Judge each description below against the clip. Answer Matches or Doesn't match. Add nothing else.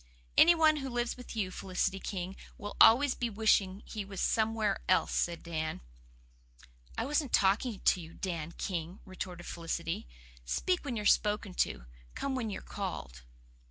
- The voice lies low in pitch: Doesn't match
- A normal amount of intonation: Matches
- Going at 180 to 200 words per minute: Doesn't match